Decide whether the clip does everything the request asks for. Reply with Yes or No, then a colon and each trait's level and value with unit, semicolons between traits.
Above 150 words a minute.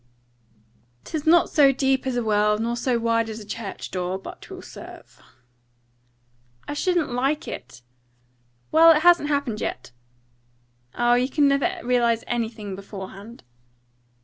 No: average, 140 wpm